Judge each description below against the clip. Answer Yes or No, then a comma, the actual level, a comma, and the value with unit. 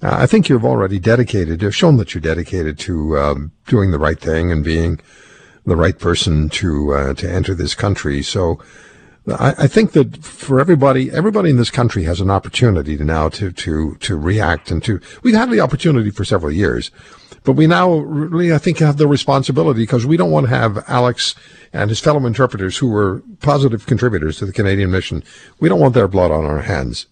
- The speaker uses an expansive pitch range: Yes, wide, 8.8 semitones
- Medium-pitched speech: No, low, 105 Hz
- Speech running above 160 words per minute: Yes, fast, 205 wpm